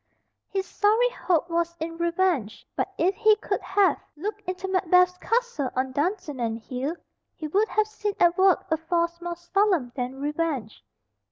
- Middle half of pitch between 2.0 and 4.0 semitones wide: No, average, 4.6 semitones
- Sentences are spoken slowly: No, average, 160 wpm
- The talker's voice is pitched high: Yes, very high, 345 Hz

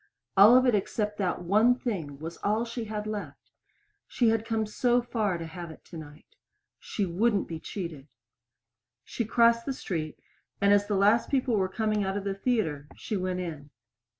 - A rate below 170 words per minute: No, average, 185 wpm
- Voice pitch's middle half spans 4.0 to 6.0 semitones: Yes, average, 4.4 semitones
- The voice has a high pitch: Yes, high, 205 Hz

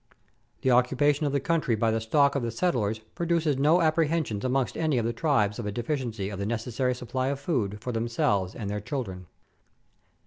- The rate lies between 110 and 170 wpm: No, average, 195 wpm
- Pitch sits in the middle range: No, low, 125 Hz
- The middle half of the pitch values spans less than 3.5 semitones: No, average, 4.7 semitones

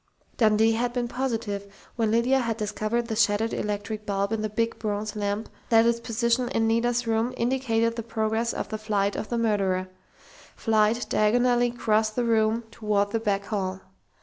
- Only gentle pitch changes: Yes, narrow, 1.8 semitones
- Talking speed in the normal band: Yes, average, 175 wpm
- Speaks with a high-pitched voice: Yes, high, 225 Hz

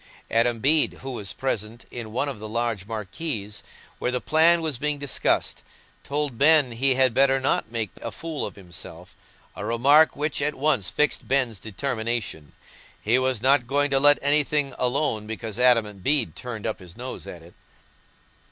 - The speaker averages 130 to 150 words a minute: No, average, 170 wpm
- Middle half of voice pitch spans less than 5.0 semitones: Yes, average, 4.4 semitones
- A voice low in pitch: Yes, low, 125 Hz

